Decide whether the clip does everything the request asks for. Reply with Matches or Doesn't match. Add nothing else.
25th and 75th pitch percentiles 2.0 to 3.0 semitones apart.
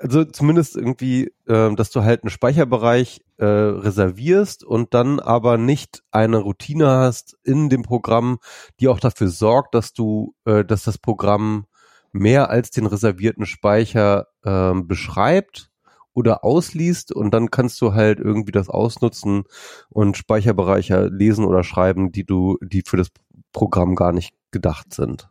Doesn't match